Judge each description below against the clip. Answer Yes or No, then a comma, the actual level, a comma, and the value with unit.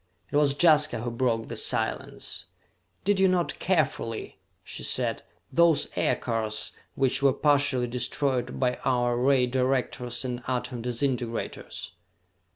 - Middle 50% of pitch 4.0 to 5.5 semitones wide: No, average, 2.8 semitones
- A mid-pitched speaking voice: No, low, 130 Hz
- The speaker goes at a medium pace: No, slow, 125 wpm